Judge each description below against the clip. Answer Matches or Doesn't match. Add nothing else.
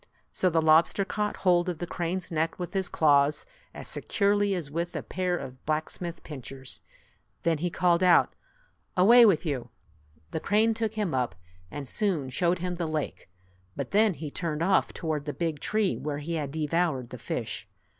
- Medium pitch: Matches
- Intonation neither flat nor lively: Matches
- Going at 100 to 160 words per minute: Doesn't match